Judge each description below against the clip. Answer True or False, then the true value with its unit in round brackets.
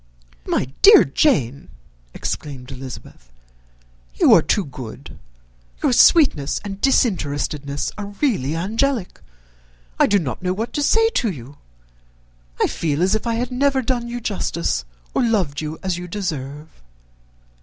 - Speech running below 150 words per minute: True (140 wpm)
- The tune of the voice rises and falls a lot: True (8.8 semitones)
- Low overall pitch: False (185 Hz)